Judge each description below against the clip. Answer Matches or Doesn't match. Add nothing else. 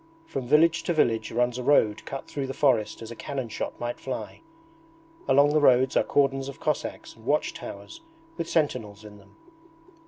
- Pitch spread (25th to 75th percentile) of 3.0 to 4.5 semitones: Matches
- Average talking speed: Matches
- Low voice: Matches